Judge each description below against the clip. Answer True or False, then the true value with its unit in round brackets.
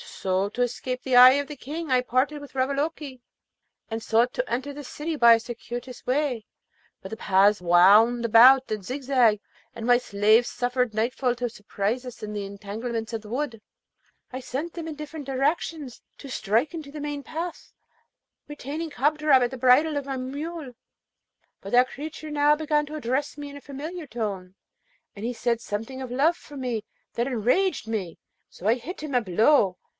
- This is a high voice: True (255 Hz)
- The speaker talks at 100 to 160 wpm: False (185 wpm)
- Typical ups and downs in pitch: True (4.3 semitones)